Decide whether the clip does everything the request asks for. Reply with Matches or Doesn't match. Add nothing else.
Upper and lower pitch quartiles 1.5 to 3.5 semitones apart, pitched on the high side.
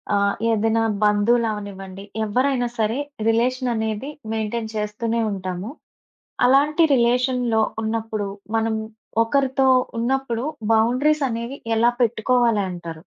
Matches